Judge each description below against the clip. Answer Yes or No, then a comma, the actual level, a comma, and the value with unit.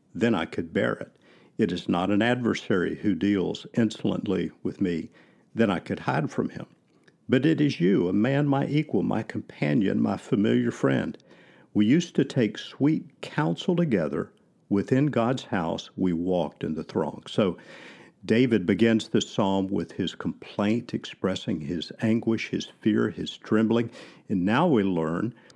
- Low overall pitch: Yes, low, 110 Hz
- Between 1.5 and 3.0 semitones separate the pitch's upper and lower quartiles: No, average, 4.3 semitones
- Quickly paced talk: No, average, 160 wpm